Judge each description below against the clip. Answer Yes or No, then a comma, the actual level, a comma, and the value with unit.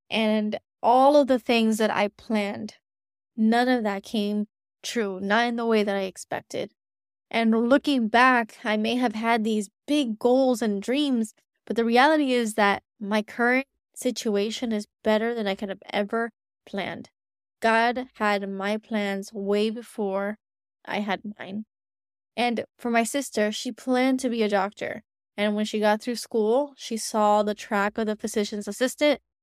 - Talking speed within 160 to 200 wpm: Yes, average, 165 wpm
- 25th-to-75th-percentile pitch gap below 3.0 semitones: Yes, narrow, 2.6 semitones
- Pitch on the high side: Yes, high, 220 Hz